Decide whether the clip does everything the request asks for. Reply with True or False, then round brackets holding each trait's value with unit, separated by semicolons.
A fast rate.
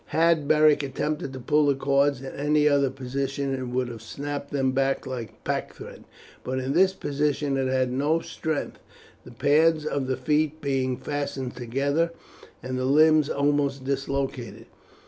False (160 wpm)